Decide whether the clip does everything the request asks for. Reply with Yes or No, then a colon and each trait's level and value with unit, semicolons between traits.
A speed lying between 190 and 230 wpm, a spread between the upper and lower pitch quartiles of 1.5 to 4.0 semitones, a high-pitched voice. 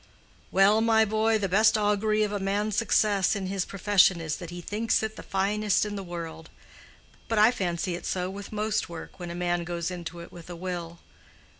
Yes: fast, 205 wpm; average, 3.4 semitones; high, 195 Hz